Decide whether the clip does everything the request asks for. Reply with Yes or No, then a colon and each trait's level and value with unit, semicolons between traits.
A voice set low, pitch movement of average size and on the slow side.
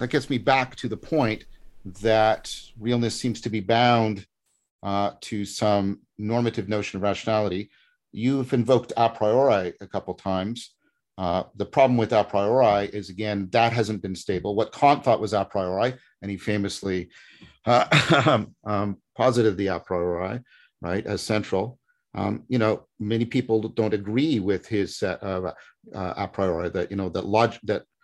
No: low, 110 Hz; average, 3.3 semitones; average, 165 wpm